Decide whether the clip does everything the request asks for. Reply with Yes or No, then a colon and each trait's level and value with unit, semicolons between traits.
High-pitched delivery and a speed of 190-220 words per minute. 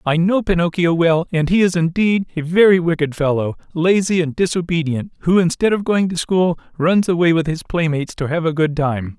No: medium, 170 Hz; fast, 205 wpm